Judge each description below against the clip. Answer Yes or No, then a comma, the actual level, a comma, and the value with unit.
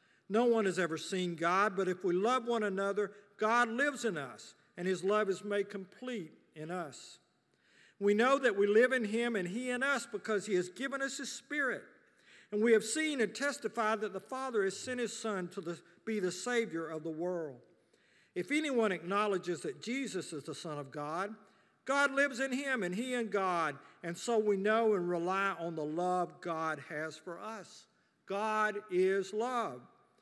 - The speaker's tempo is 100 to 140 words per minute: No, average, 195 wpm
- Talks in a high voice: Yes, high, 205 Hz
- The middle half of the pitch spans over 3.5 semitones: Yes, average, 4.6 semitones